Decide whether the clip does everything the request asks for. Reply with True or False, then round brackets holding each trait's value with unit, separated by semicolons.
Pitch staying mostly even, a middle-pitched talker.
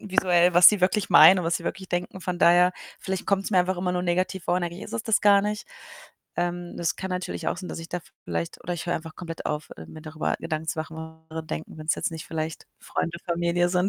True (2.2 semitones; 175 Hz)